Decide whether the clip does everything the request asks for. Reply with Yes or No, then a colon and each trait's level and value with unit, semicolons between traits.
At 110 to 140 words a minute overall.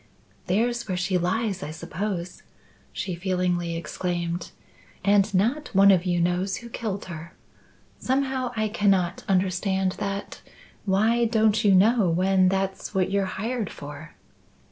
Yes: slow, 135 wpm